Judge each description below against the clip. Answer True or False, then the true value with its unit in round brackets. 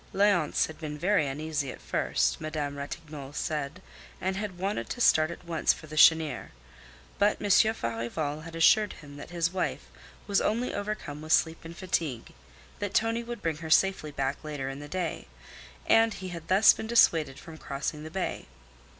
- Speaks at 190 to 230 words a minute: False (180 wpm)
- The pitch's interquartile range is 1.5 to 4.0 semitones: False (4.5 semitones)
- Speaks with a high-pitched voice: False (160 Hz)